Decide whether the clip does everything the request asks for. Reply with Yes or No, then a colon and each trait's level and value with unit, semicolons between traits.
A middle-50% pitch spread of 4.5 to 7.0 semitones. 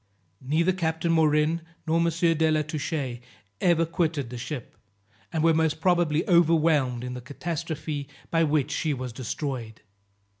No: average, 2.9 semitones